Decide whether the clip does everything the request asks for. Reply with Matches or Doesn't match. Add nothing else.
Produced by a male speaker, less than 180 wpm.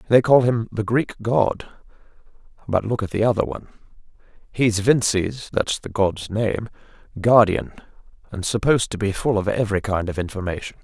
Matches